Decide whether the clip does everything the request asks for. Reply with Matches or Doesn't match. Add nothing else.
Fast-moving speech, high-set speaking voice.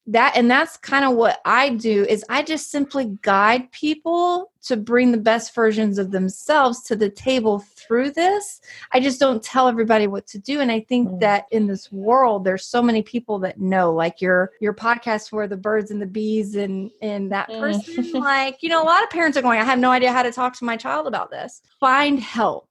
Matches